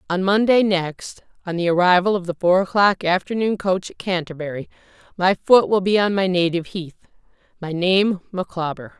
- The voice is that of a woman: Yes, female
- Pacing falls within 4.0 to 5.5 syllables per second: Yes, 5.1 syllables/s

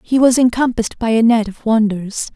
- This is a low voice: No, high, 230 Hz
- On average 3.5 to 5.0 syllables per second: No, 5.4 syllables/s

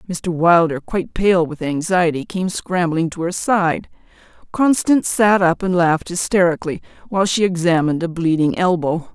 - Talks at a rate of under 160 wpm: Yes, average, 150 wpm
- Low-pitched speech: No, medium, 175 Hz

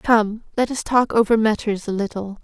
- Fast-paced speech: No, average, 195 wpm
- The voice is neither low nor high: No, high, 220 Hz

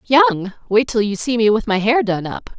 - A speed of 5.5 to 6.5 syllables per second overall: No, 5.3 syllables/s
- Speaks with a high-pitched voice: Yes, high, 225 Hz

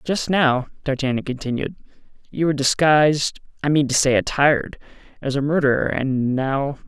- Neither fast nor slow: No, slow, 130 wpm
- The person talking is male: Yes, male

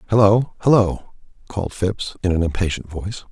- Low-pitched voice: Yes, low, 100 Hz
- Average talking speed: Yes, average, 145 wpm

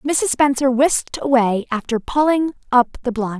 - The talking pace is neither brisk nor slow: Yes, average, 160 wpm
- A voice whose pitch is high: Yes, very high, 260 Hz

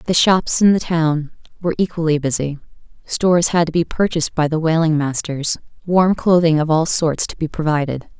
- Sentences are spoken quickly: No, average, 185 wpm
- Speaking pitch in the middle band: Yes, medium, 160 Hz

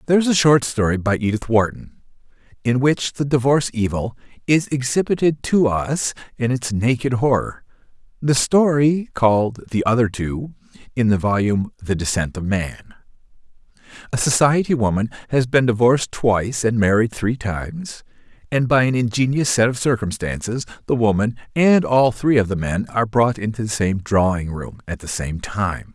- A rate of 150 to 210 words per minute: Yes, average, 165 wpm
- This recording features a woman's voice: No, male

